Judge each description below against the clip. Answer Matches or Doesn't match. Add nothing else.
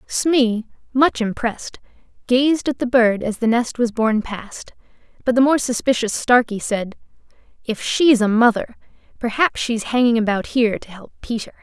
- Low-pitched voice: Doesn't match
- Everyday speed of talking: Matches